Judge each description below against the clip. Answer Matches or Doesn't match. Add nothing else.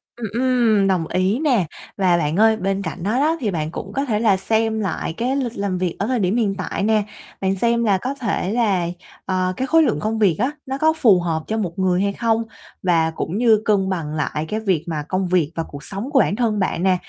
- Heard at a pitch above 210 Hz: Doesn't match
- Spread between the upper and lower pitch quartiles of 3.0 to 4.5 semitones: Matches